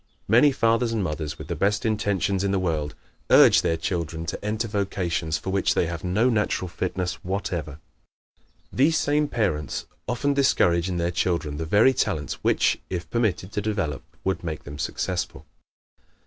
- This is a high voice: No, very low, 95 Hz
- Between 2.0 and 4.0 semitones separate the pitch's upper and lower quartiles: No, average, 4.4 semitones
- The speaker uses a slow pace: No, average, 165 wpm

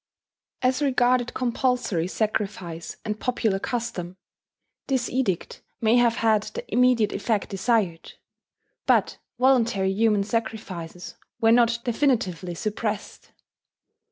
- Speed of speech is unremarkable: No, slow, 100 wpm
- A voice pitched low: No, high, 225 Hz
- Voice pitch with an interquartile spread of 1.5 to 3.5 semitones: No, average, 3.9 semitones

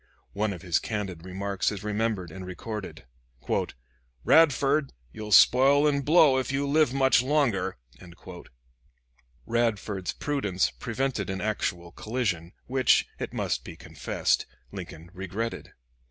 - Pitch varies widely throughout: Yes, wide, 6.0 semitones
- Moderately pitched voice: No, low, 110 Hz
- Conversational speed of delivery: No, slow, 120 wpm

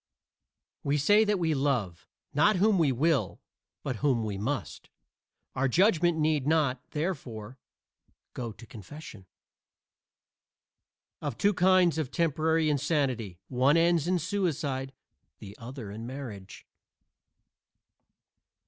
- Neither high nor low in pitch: Yes, medium, 145 Hz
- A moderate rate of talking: No, slow, 110 wpm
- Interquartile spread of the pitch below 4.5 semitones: No, wide, 5.4 semitones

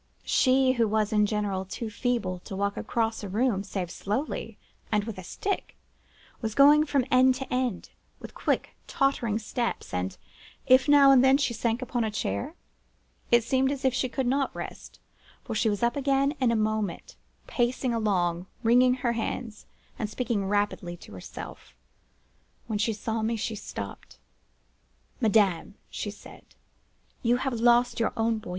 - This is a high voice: Yes, high, 230 Hz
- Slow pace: No, average, 165 wpm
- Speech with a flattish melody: No, average, 3.7 semitones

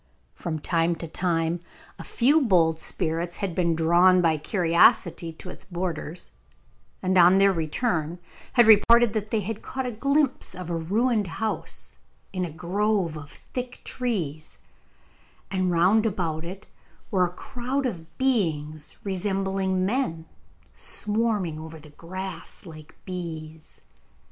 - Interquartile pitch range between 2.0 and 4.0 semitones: No, average, 4.4 semitones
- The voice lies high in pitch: No, medium, 180 Hz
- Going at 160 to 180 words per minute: No, slow, 135 wpm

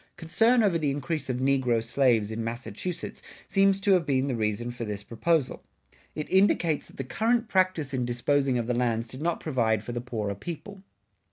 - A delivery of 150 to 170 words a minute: No, average, 195 wpm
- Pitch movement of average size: No, wide, 6.3 semitones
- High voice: No, low, 135 Hz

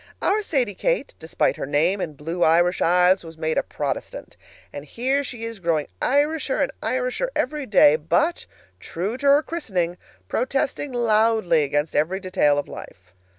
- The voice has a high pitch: Yes, high, 195 Hz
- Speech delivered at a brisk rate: No, average, 160 wpm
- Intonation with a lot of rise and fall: Yes, wide, 8.6 semitones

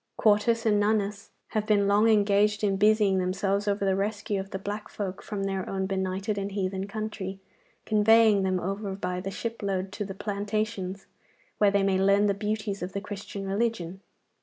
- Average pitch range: No, narrow, 1.5 semitones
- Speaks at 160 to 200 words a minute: Yes, average, 180 wpm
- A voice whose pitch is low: No, high, 200 Hz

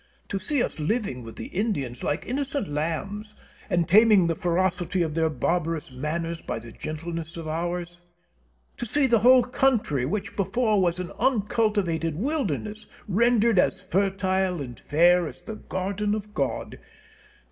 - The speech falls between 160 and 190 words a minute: No, average, 150 wpm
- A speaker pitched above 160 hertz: Yes, medium, 185 Hz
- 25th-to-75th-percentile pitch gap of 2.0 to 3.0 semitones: No, average, 4.6 semitones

